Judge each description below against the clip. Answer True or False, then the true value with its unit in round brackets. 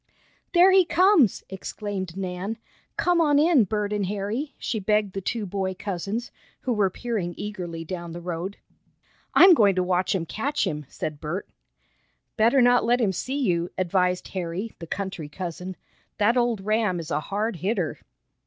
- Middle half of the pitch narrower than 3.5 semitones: False (4.4 semitones)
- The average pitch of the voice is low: False (200 Hz)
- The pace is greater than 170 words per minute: False (165 wpm)